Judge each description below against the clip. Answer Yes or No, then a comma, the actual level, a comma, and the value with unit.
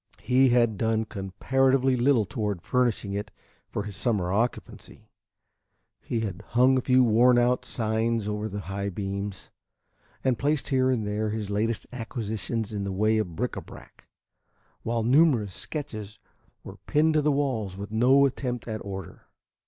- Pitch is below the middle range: Yes, low, 110 Hz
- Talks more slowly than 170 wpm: Yes, average, 160 wpm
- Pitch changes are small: No, average, 3.6 semitones